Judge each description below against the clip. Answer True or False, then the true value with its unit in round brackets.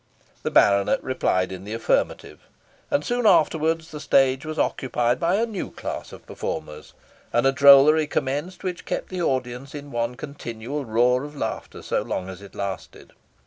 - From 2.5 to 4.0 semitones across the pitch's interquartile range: False (4.8 semitones)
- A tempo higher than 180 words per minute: False (170 wpm)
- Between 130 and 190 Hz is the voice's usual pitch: True (135 Hz)